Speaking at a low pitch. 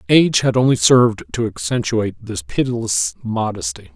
Yes: low, 110 Hz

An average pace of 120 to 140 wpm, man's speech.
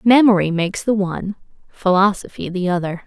No: slow, 135 wpm; female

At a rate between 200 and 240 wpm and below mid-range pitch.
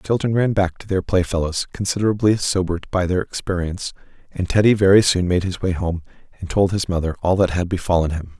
Yes: fast, 205 wpm; very low, 90 Hz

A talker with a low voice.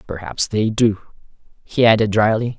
Yes: low, 110 Hz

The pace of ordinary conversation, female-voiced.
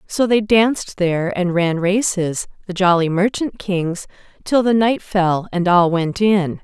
Yes: average, 170 wpm; female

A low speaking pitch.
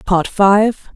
No: high, 200 Hz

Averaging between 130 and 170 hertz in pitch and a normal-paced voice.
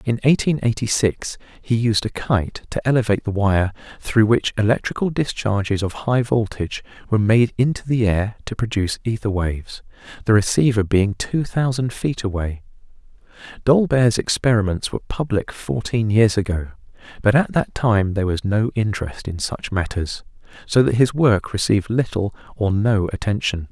No: low, 110 Hz; average, 155 wpm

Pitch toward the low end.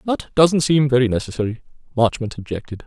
Yes: low, 130 Hz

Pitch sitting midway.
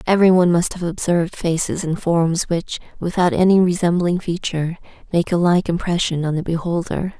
Yes: medium, 175 Hz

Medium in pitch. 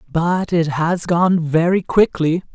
Yes: medium, 170 Hz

